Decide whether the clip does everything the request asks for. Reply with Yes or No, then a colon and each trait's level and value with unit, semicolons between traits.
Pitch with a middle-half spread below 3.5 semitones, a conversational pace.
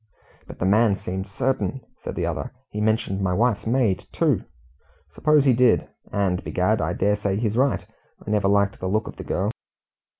Yes: average, 3.1 semitones; average, 190 wpm